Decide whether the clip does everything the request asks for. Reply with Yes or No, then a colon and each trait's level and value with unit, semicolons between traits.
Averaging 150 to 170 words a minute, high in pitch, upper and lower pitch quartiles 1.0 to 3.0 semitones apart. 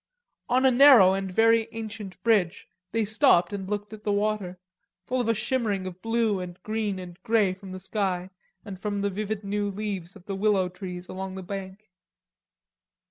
No: average, 185 wpm; high, 200 Hz; narrow, 2.6 semitones